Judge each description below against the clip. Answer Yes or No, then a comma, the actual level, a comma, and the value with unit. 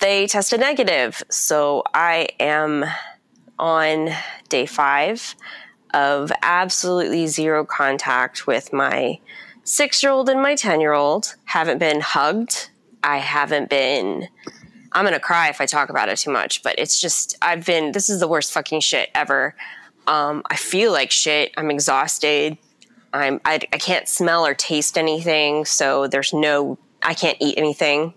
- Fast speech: No, average, 145 wpm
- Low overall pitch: No, medium, 155 Hz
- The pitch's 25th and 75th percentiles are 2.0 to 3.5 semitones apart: Yes, average, 3.2 semitones